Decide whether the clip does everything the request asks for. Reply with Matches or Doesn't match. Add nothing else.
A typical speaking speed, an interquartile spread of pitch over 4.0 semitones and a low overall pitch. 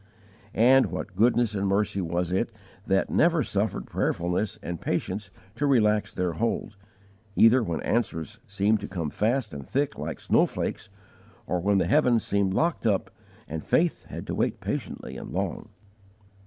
Matches